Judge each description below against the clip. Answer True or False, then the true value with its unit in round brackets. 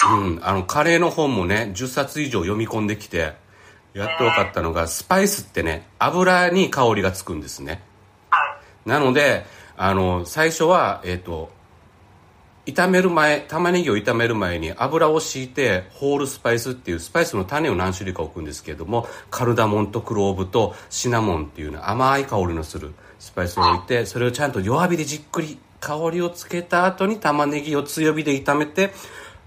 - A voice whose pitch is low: True (115 Hz)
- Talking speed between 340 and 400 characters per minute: True (355 characters per minute)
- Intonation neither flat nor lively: False (8.0 semitones)